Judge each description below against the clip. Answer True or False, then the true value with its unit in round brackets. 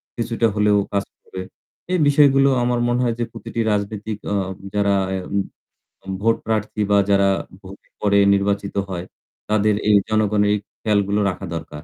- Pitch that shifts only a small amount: True (2.2 semitones)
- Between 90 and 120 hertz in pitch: True (105 Hz)